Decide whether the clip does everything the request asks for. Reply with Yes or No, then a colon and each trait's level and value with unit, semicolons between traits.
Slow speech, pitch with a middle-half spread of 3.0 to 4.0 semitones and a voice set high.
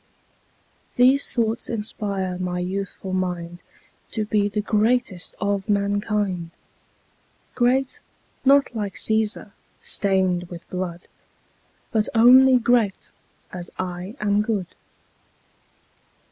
Yes: slow, 95 wpm; average, 3.4 semitones; high, 205 Hz